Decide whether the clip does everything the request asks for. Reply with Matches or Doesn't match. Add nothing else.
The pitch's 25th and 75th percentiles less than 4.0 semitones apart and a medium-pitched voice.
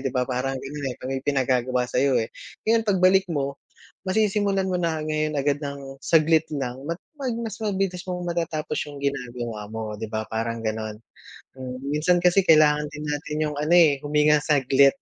Doesn't match